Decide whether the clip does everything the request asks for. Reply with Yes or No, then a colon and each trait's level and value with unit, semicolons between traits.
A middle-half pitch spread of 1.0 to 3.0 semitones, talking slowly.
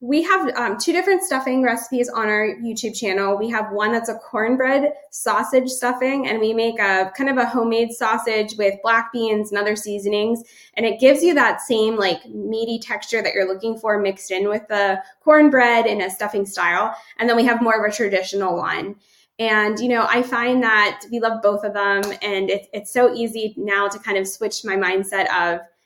No: narrow, 2.6 semitones; fast, 205 wpm